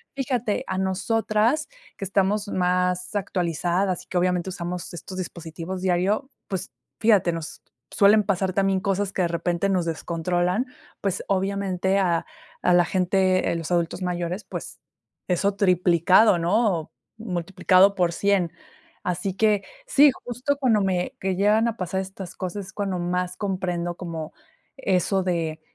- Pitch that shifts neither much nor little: No, narrow, 2.3 semitones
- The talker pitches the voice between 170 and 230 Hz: Yes, medium, 185 Hz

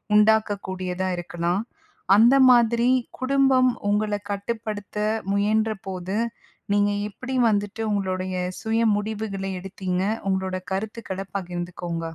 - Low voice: No, high, 205 Hz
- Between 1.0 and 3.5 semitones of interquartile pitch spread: Yes, average, 2.8 semitones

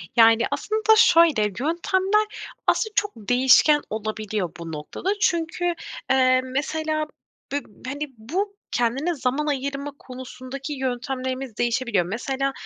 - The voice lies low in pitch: No, very high, 265 Hz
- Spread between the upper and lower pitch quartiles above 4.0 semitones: Yes, average, 4.7 semitones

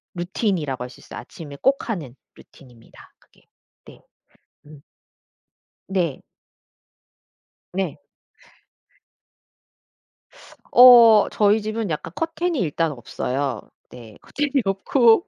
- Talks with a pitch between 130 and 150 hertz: No, high, 190 Hz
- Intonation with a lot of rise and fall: Yes, wide, 8.4 semitones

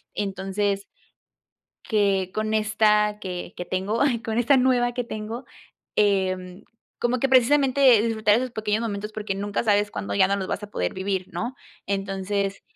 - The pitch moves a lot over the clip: No, average, 2.8 semitones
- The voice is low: No, high, 210 Hz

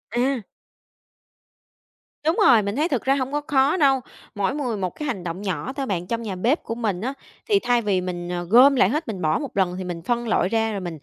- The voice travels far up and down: Yes, wide, 6.2 semitones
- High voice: Yes, high, 230 Hz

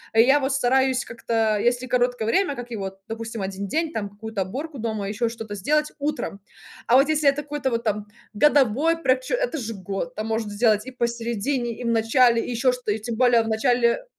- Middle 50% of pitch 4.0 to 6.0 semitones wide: No, average, 3.3 semitones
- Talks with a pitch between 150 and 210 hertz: No, high, 235 Hz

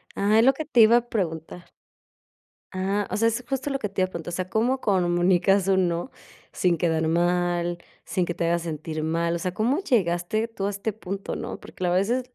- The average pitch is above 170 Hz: Yes, medium, 185 Hz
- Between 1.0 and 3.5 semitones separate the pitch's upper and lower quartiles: No, average, 4.2 semitones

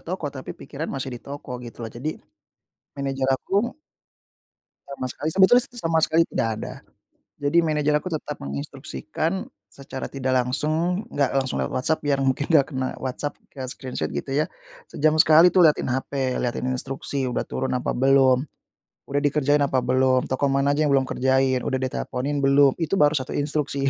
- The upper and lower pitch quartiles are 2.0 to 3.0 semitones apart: Yes, average, 2.7 semitones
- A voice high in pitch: No, medium, 140 Hz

